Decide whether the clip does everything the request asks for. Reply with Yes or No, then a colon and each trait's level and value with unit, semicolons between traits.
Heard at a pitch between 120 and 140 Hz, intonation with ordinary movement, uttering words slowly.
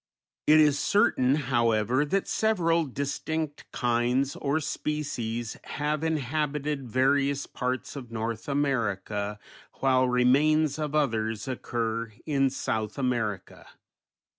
Yes: low, 135 Hz; average, 4.1 semitones; slow, 105 wpm